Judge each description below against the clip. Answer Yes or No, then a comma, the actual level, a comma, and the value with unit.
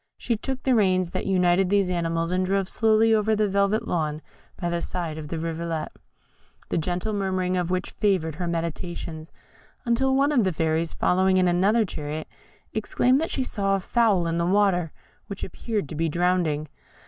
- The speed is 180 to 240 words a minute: Yes, average, 185 wpm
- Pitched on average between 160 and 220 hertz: Yes, medium, 185 Hz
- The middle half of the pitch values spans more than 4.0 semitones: No, average, 3.7 semitones